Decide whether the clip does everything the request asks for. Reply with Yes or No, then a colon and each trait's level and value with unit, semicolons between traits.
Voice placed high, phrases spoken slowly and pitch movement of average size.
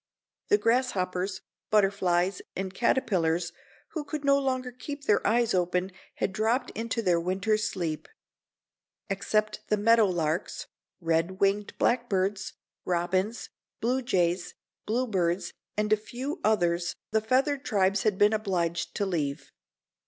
Yes: high, 200 Hz; slow, 125 wpm; average, 4.3 semitones